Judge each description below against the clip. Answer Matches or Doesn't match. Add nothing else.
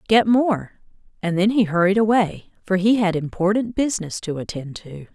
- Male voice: Doesn't match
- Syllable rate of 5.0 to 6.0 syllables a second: Matches